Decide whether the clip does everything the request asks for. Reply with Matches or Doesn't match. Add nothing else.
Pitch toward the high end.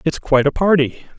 Doesn't match